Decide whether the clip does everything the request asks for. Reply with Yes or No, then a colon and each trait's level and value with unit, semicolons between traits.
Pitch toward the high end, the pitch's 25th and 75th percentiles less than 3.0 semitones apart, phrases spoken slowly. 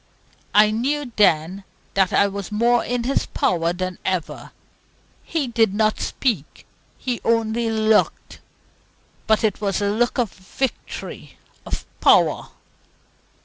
No: high, 215 Hz; average, 3.4 semitones; slow, 125 wpm